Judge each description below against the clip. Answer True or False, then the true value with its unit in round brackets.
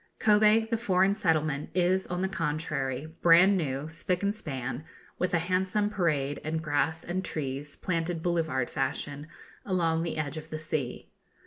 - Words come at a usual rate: True (155 wpm)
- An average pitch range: True (3.9 semitones)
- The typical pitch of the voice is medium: True (165 Hz)